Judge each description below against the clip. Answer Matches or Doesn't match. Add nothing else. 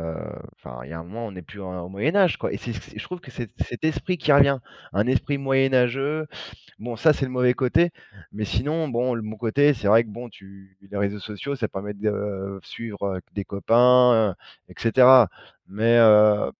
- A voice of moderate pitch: Doesn't match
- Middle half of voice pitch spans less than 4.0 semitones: Doesn't match